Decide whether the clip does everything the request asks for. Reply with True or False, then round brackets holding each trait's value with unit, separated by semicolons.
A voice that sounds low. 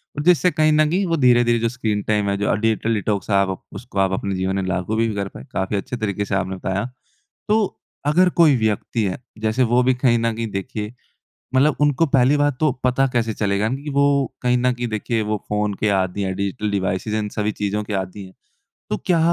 True (110 Hz)